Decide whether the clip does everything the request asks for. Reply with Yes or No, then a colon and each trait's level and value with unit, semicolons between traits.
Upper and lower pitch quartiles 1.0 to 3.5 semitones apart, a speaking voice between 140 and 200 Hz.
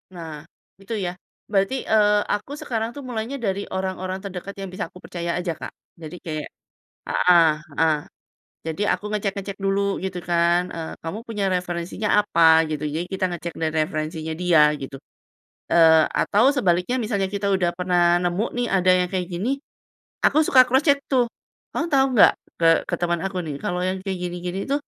Yes: average, 3.2 semitones; medium, 185 Hz